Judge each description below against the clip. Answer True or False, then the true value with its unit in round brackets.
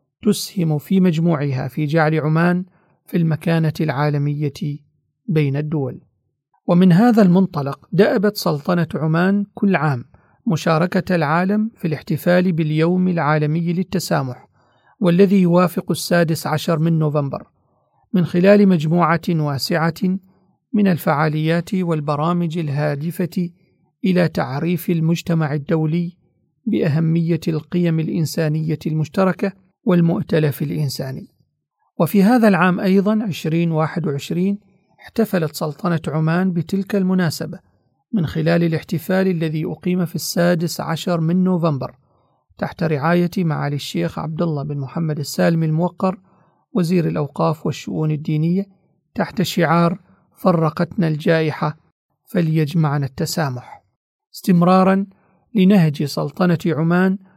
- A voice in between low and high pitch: True (170 Hz)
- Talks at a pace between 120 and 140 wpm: False (100 wpm)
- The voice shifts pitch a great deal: False (2.9 semitones)